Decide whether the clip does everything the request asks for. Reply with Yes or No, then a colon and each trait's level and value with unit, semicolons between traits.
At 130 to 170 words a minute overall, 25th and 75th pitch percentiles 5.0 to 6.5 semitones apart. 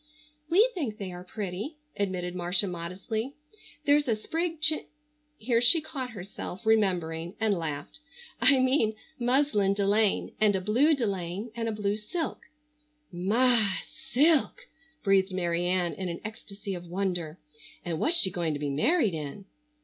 Yes: average, 150 wpm; wide, 5.4 semitones